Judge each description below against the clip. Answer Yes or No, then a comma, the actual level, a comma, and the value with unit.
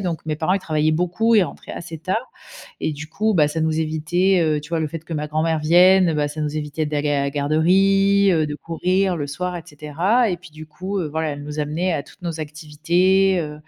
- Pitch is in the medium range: Yes, medium, 160 Hz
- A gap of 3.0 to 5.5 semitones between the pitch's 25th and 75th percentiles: Yes, average, 3.3 semitones